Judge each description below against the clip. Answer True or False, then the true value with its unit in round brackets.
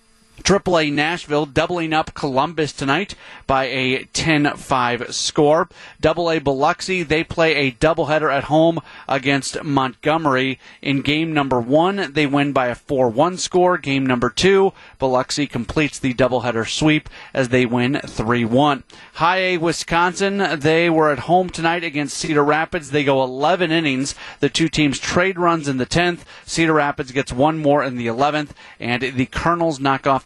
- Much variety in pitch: False (3.6 semitones)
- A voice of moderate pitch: True (150 Hz)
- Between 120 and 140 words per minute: False (165 wpm)